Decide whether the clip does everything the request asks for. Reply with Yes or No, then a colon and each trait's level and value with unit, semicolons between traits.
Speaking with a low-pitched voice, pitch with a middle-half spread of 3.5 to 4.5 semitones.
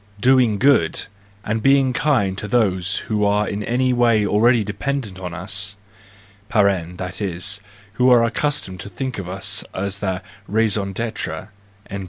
Yes: low, 105 Hz; average, 4.1 semitones